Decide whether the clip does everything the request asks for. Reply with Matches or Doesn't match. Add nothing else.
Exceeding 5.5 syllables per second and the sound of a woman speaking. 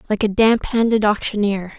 Doesn't match